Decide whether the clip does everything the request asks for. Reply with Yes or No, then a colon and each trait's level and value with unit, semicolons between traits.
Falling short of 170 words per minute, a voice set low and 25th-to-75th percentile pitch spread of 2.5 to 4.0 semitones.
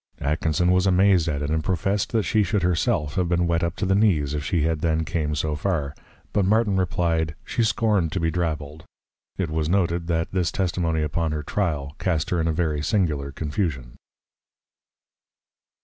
No: average, 190 wpm; very low, 85 Hz; average, 3.4 semitones